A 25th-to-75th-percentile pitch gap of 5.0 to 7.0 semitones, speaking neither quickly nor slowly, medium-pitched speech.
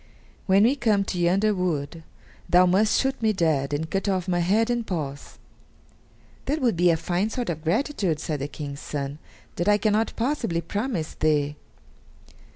Yes: wide, 5.4 semitones; average, 170 wpm; medium, 180 Hz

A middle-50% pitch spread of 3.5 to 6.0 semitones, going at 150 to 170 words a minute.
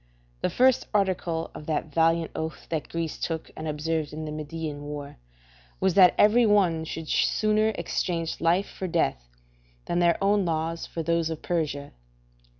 No: narrow, 2.5 semitones; average, 160 wpm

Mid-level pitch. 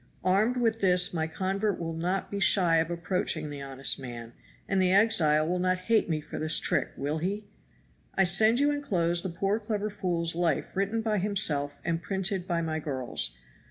Yes: medium, 180 Hz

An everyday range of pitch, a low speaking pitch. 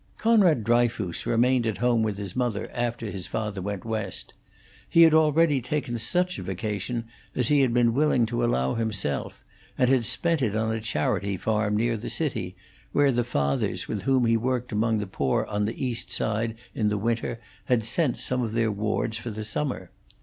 Yes: average, 3.0 semitones; low, 115 Hz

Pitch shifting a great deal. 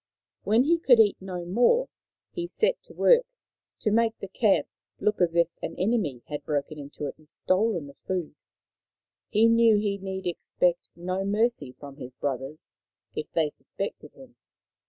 Yes: wide, 6.6 semitones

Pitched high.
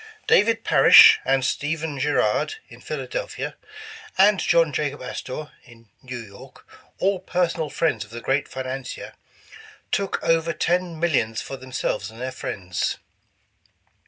No: medium, 145 Hz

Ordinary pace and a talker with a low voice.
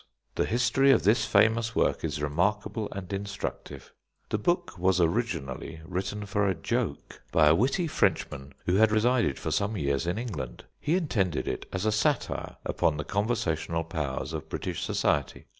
Yes: average, 165 wpm; low, 100 Hz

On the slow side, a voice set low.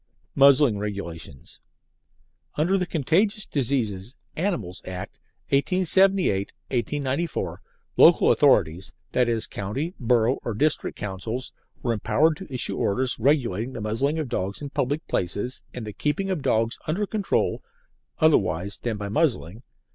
Yes: slow, 125 wpm; low, 125 Hz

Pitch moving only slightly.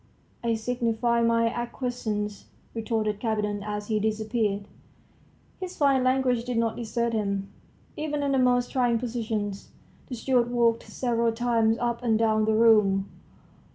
Yes: narrow, 2.1 semitones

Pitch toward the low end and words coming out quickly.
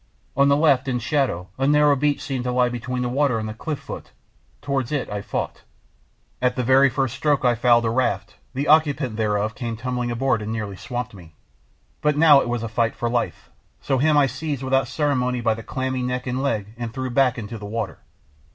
Yes: low, 125 Hz; fast, 215 wpm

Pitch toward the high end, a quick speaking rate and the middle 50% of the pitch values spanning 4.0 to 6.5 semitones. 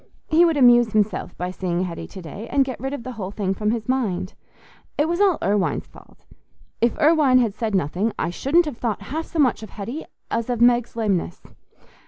Yes: high, 230 Hz; fast, 210 wpm; average, 5.2 semitones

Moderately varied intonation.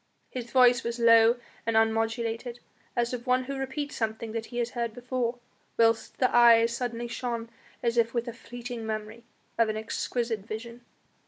No: narrow, 1.3 semitones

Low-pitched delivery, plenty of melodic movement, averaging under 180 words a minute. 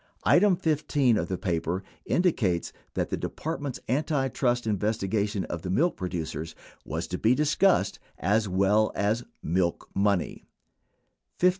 Yes: low, 110 Hz; wide, 7.2 semitones; average, 140 wpm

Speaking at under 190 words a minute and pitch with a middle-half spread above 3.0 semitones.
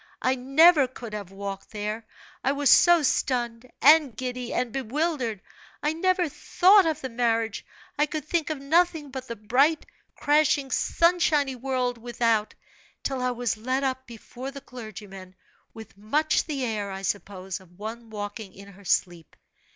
Yes: average, 160 wpm; average, 5.1 semitones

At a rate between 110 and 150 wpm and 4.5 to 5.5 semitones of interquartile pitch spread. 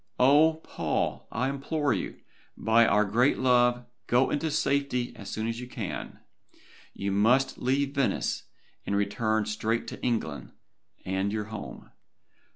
No: average, 140 wpm; average, 3.9 semitones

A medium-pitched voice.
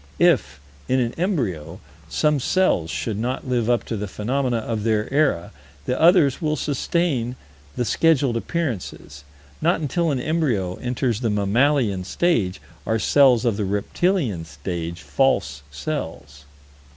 No: low, 120 Hz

